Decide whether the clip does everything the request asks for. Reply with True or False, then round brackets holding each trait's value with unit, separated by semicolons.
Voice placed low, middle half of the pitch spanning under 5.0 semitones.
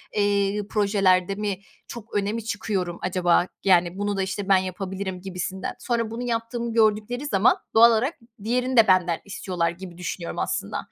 False (200 Hz; 3.4 semitones)